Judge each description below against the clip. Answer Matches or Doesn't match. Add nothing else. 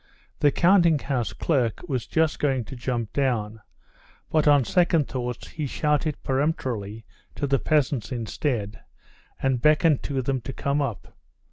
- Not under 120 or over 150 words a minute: Matches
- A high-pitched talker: Doesn't match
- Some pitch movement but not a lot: Matches